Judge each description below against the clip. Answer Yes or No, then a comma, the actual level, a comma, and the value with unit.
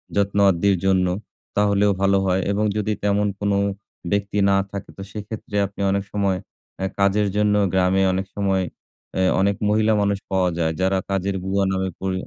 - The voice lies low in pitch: Yes, low, 100 Hz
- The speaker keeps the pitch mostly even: Yes, narrow, 1.2 semitones